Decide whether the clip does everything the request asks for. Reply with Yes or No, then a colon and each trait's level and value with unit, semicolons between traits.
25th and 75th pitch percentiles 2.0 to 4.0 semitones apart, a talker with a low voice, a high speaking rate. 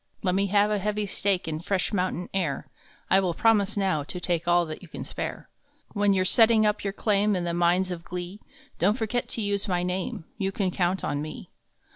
No: narrow, 2.6 semitones; high, 190 Hz; fast, 225 wpm